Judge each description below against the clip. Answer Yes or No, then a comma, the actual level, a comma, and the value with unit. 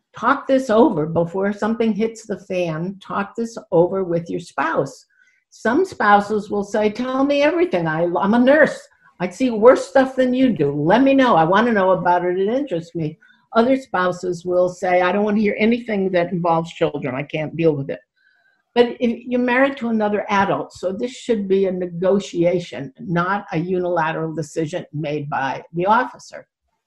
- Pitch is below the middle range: No, high, 200 Hz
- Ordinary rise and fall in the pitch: No, wide, 5.8 semitones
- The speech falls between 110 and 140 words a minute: No, average, 185 wpm